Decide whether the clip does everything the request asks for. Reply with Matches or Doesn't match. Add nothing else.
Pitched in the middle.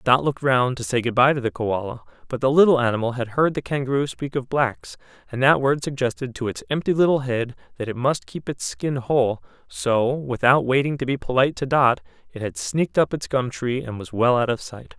Doesn't match